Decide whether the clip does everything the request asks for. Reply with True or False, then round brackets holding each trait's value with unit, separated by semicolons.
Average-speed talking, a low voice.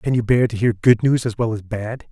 False (310 wpm; 115 Hz)